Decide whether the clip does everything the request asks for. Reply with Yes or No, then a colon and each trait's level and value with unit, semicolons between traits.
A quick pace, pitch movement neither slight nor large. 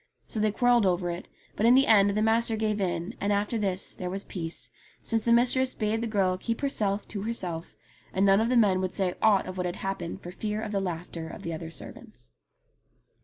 Yes: fast, 225 wpm; average, 3.4 semitones